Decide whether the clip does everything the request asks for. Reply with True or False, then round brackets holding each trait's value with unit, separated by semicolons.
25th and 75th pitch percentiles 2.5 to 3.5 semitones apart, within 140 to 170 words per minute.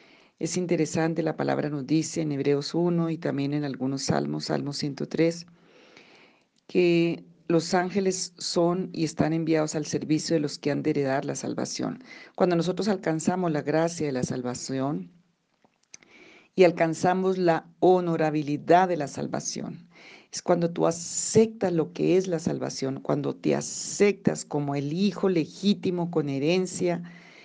True (3.1 semitones; 145 wpm)